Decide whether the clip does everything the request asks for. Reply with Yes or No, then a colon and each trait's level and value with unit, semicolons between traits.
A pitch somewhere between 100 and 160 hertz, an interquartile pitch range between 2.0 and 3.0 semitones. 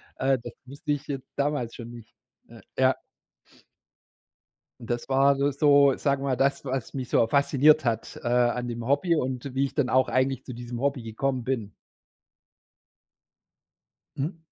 Yes: low, 135 Hz; narrow, 2.5 semitones